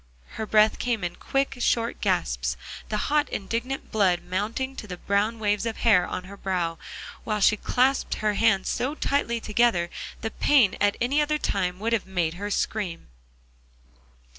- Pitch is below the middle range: No, high, 210 Hz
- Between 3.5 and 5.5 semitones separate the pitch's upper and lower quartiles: Yes, average, 3.9 semitones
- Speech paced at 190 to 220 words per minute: No, average, 165 wpm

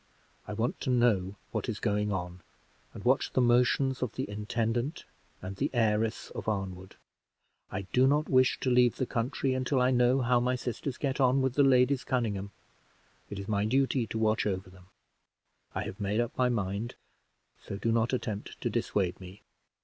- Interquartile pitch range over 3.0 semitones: Yes, average, 3.9 semitones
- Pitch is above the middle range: No, low, 115 Hz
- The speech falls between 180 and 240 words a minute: Yes, average, 190 wpm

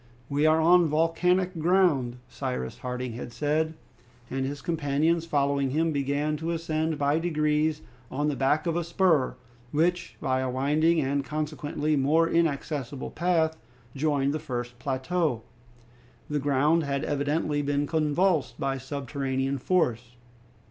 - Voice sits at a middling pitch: Yes, medium, 150 Hz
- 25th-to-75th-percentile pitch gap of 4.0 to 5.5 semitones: No, average, 3.0 semitones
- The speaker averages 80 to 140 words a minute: Yes, slow, 135 wpm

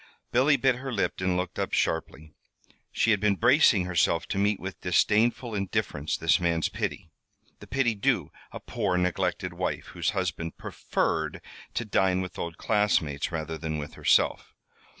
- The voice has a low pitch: Yes, very low, 95 Hz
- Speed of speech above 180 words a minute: No, average, 160 wpm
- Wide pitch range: No, average, 4.5 semitones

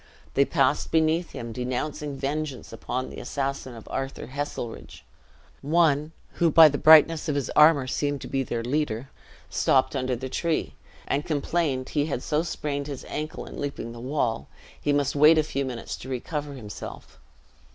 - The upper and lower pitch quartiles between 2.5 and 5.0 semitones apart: Yes, average, 2.8 semitones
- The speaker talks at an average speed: Yes, average, 170 wpm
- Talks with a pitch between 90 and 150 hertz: Yes, medium, 140 Hz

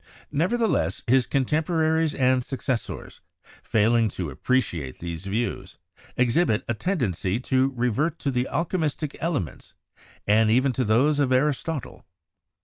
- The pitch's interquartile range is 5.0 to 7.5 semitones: Yes, average, 5.3 semitones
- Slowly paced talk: Yes, slow, 130 wpm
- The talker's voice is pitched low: Yes, low, 130 Hz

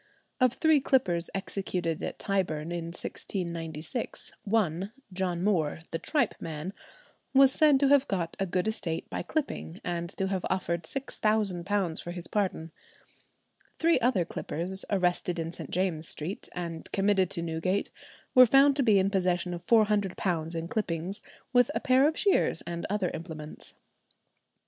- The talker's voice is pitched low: No, medium, 185 Hz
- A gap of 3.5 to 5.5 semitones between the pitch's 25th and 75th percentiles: Yes, average, 4.2 semitones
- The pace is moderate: Yes, average, 150 wpm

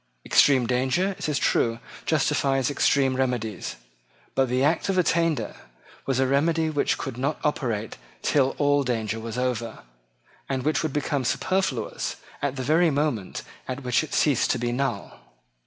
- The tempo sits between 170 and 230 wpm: No, average, 155 wpm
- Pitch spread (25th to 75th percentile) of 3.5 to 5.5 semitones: No, average, 3.1 semitones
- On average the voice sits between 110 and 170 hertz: Yes, low, 135 Hz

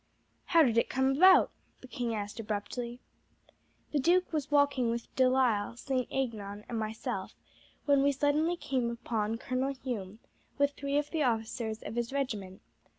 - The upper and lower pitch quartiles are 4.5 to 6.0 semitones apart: No, average, 3.9 semitones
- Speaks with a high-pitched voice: Yes, very high, 255 Hz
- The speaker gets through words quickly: No, average, 160 wpm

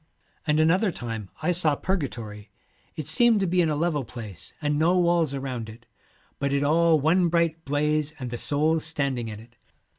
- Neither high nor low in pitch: Yes, medium, 150 Hz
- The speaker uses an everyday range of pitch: Yes, average, 4.9 semitones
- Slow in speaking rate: No, average, 185 wpm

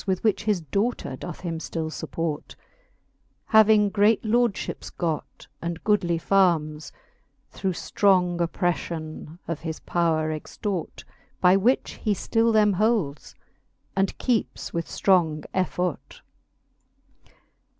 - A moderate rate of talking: No, slow, 115 wpm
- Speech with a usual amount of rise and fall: Yes, average, 4.2 semitones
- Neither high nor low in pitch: Yes, medium, 180 Hz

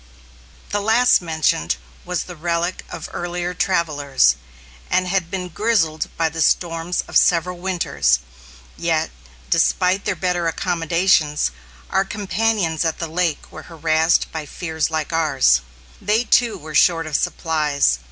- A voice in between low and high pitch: Yes, medium, 170 Hz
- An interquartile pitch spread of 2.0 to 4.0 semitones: Yes, narrow, 2.5 semitones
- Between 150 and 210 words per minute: No, slow, 135 wpm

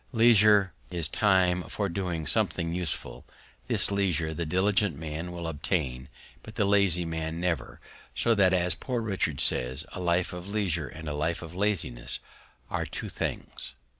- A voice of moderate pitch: No, very low, 90 Hz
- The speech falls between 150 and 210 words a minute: Yes, average, 160 wpm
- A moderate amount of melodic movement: Yes, average, 3.7 semitones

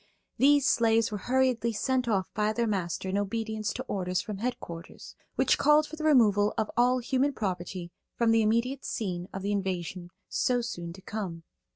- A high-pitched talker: Yes, high, 215 Hz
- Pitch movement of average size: Yes, average, 4.6 semitones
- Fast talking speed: No, average, 180 wpm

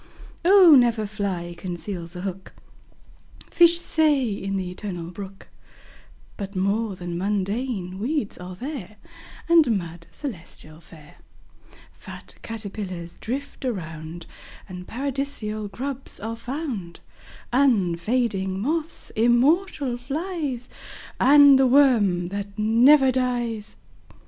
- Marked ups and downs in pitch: Yes, wide, 6.2 semitones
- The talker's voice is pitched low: No, high, 215 Hz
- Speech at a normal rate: No, slow, 105 wpm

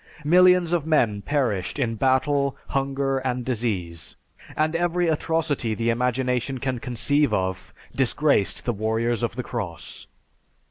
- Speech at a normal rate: No, slow, 130 wpm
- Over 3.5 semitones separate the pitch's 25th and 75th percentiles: Yes, average, 4.2 semitones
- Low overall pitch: Yes, low, 130 Hz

